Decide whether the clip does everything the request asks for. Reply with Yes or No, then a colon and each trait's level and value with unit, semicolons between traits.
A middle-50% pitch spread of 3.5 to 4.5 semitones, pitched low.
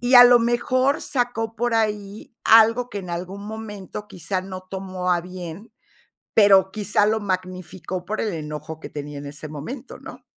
No: average, 3.8 semitones; high, 200 Hz